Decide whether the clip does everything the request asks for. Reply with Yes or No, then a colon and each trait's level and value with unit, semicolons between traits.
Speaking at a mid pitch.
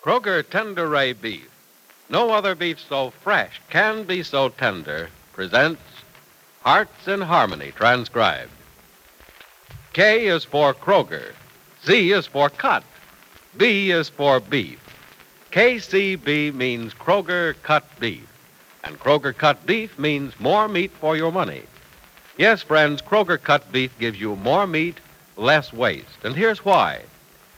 Yes: medium, 155 Hz